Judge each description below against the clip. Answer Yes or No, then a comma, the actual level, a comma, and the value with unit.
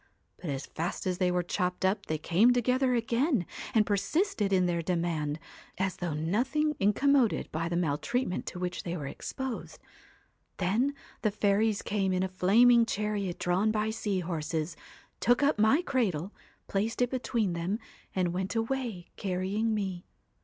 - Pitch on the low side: No, high, 200 Hz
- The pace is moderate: Yes, average, 160 wpm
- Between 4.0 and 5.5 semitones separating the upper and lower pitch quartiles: Yes, average, 4.6 semitones